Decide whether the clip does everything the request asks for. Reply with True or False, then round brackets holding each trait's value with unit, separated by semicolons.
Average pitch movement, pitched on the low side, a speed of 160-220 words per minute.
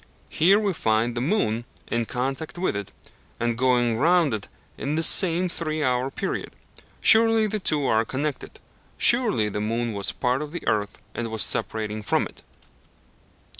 False (7.0 semitones; 130 Hz; 170 wpm)